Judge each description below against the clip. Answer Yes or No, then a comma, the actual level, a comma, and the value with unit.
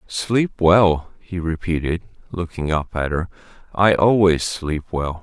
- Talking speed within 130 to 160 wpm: Yes, average, 140 wpm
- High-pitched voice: No, very low, 85 Hz